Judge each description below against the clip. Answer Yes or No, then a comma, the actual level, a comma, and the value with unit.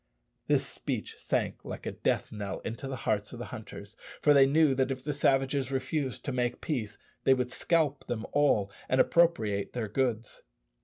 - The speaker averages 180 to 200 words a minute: Yes, average, 185 wpm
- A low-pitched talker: Yes, low, 130 Hz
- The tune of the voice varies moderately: Yes, average, 3.9 semitones